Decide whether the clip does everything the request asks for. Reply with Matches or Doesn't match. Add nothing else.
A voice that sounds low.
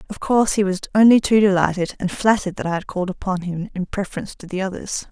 Doesn't match